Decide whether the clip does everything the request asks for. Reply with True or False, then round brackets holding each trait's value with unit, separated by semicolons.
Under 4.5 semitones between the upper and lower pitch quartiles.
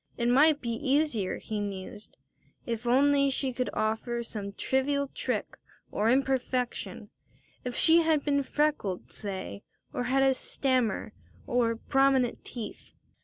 True (3.5 semitones)